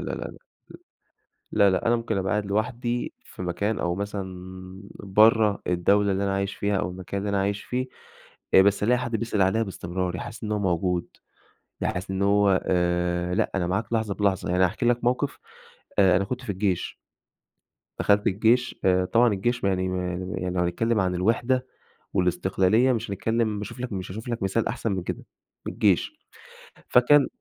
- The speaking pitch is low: Yes, low, 100 Hz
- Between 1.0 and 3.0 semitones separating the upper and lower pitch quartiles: No, average, 3.4 semitones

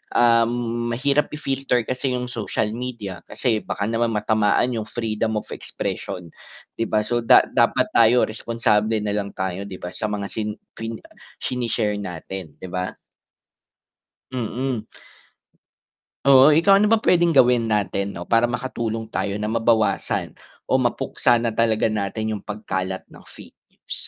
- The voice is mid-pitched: No, low, 115 Hz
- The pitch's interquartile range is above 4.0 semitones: No, average, 2.7 semitones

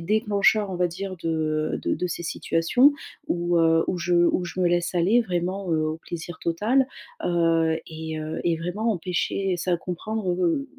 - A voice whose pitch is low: No, medium, 175 Hz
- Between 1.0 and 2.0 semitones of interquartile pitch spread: No, average, 2.8 semitones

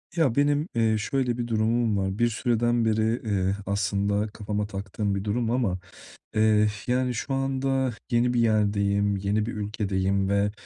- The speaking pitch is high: No, low, 110 Hz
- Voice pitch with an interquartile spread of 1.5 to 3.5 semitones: Yes, average, 2.9 semitones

